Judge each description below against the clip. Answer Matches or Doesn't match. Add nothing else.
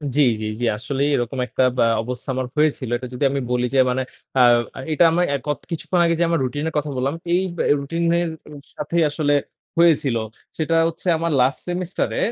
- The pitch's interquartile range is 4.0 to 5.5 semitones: Matches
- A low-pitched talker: Doesn't match